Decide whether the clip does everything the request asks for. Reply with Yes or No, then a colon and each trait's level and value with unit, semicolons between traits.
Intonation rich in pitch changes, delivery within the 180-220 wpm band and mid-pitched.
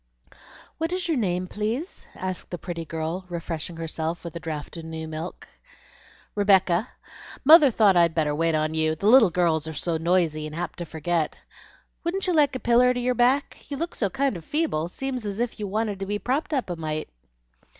Yes: wide, 7.2 semitones; average, 200 wpm; medium, 180 Hz